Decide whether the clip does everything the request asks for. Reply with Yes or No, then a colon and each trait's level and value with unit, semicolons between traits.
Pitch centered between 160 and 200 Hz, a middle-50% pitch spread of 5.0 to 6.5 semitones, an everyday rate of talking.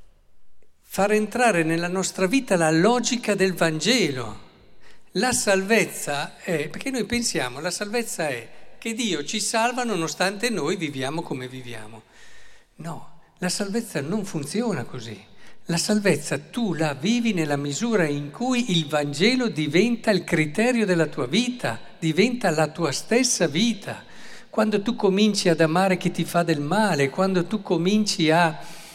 Yes: medium, 185 Hz; wide, 5.4 semitones; average, 145 wpm